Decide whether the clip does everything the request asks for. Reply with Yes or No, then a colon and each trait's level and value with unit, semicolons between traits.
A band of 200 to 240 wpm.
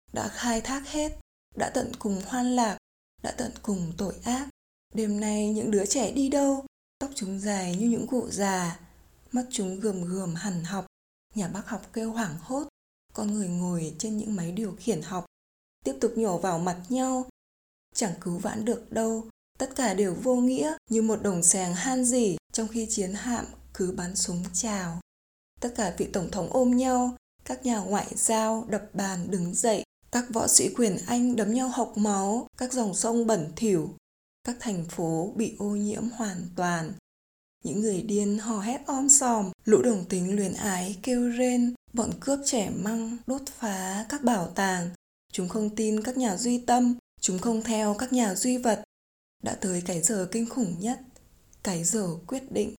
No: average, 185 wpm